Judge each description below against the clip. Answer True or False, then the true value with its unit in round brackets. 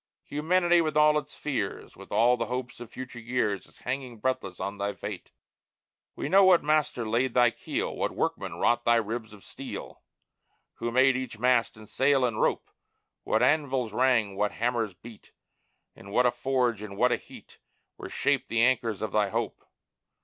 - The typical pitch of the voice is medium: False (120 Hz)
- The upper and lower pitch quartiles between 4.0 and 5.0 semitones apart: False (3.4 semitones)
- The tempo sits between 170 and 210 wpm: True (180 wpm)